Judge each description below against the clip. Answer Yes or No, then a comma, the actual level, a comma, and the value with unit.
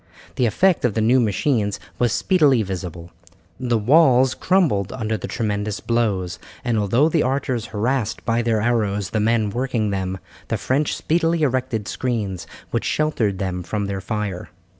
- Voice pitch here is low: Yes, low, 115 Hz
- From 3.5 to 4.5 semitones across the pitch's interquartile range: Yes, average, 4.2 semitones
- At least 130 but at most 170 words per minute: Yes, average, 160 wpm